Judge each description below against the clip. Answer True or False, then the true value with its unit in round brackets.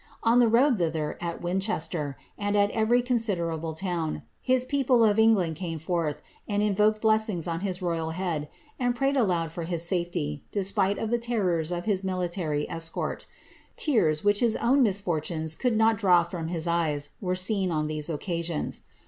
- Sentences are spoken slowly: False (170 wpm)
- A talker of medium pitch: True (180 Hz)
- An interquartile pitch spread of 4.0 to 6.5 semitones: True (4.8 semitones)